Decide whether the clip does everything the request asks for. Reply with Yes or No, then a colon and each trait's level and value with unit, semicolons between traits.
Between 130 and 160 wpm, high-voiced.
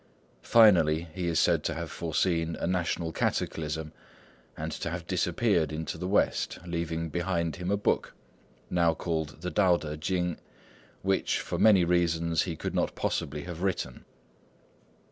No: average, 150 wpm; very low, 85 Hz